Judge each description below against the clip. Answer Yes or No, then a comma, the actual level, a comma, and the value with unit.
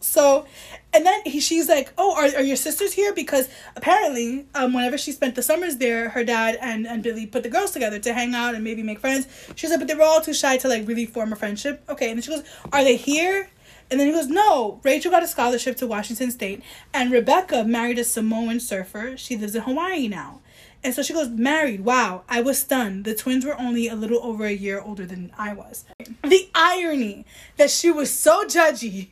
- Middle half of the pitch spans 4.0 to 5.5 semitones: Yes, average, 4.6 semitones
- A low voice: No, very high, 255 Hz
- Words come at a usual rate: No, fast, 230 wpm